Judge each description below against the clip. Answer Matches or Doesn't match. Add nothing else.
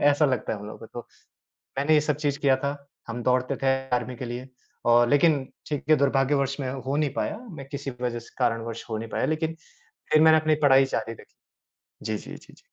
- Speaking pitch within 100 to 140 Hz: Matches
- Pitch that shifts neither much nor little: Matches